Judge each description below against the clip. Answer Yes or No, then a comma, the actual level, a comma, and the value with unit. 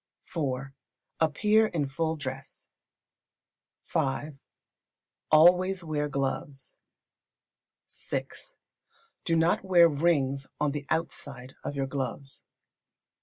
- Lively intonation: No, average, 3.5 semitones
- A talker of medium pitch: Yes, medium, 145 Hz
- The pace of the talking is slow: Yes, slow, 90 wpm